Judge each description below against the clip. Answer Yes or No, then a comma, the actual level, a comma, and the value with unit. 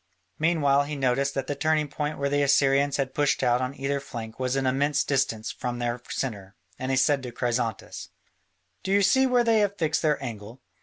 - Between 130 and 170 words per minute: No, fast, 205 wpm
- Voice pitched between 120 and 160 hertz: Yes, low, 135 Hz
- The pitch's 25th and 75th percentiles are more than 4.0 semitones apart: No, average, 3.0 semitones